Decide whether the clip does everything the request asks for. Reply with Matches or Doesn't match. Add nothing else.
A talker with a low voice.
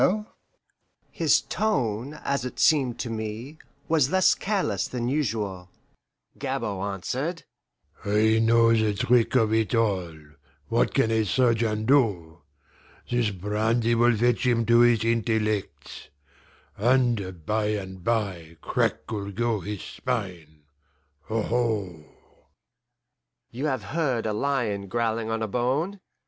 Matches